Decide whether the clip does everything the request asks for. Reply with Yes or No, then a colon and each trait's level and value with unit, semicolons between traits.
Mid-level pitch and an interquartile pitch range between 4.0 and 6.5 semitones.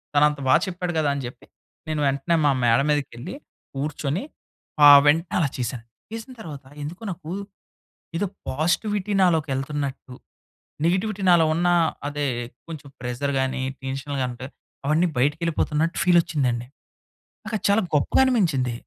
Yes: medium, 150 Hz; average, 4.4 semitones